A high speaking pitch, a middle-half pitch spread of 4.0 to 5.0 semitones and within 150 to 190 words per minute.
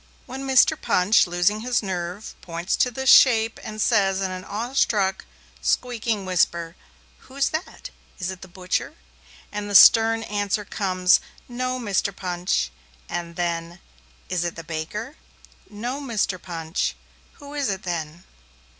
No: high, 200 Hz; average, 4.6 semitones; average, 140 wpm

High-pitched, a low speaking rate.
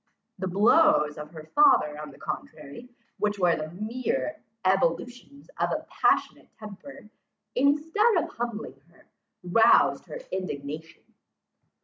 Yes: high, 205 Hz; slow, 120 wpm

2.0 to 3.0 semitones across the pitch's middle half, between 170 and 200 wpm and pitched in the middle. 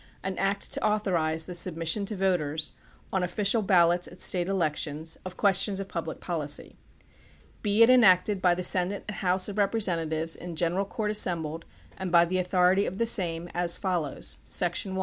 Yes: average, 2.7 semitones; average, 180 wpm; medium, 180 Hz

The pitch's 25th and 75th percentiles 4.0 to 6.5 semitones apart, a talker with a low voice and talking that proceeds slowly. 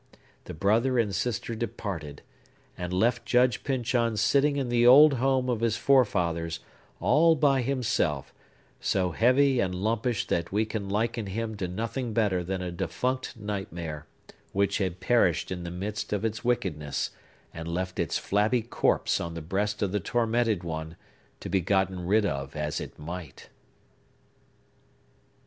No: average, 5.2 semitones; low, 105 Hz; average, 155 wpm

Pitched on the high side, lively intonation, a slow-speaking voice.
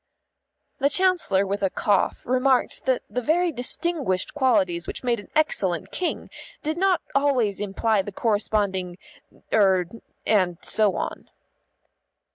Yes: high, 220 Hz; wide, 6.5 semitones; slow, 125 wpm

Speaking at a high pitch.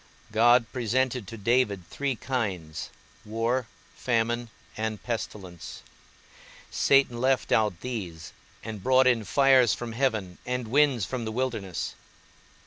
No: low, 115 Hz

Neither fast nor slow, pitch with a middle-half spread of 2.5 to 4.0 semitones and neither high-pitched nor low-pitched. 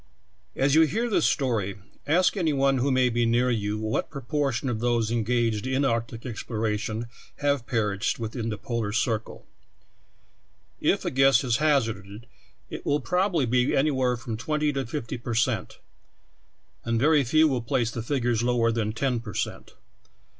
No: average, 170 wpm; average, 3.4 semitones; low, 120 Hz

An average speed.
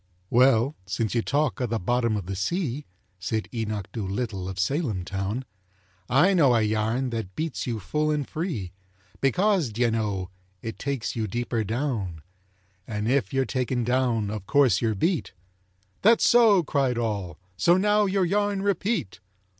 Yes: average, 155 wpm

